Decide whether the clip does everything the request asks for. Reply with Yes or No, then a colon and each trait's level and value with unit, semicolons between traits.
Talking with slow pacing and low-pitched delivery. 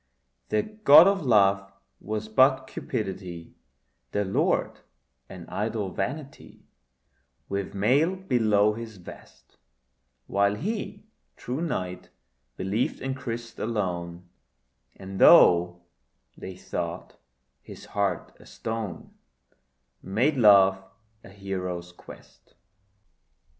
Yes: slow, 95 wpm; low, 105 Hz